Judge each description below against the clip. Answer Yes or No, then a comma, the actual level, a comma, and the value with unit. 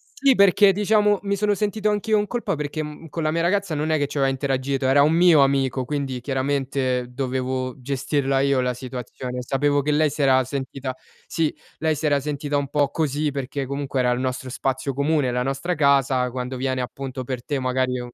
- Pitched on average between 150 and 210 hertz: No, medium, 140 Hz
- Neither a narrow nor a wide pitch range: Yes, average, 3.0 semitones